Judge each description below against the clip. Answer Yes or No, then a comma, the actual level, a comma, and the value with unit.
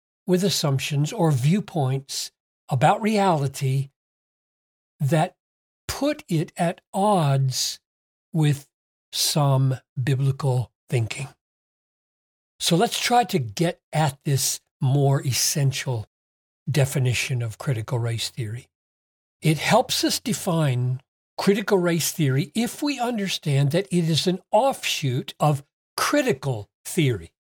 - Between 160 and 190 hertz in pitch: No, medium, 140 Hz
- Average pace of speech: No, slow, 100 wpm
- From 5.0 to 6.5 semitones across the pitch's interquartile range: Yes, wide, 5.6 semitones